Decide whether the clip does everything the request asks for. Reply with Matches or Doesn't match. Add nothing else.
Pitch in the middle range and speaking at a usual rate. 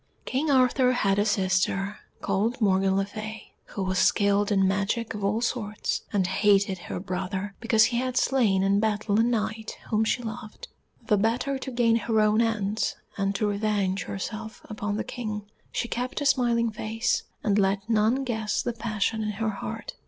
Doesn't match